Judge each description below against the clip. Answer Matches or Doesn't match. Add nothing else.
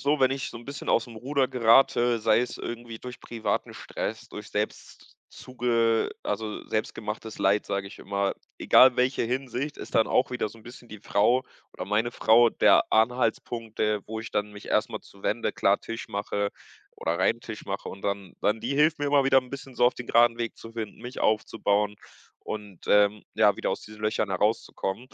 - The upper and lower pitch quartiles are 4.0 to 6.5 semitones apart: Doesn't match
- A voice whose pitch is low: Matches